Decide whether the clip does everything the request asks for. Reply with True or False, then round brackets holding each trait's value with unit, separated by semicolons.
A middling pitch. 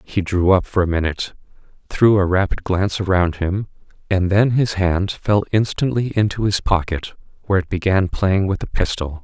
False (95 Hz)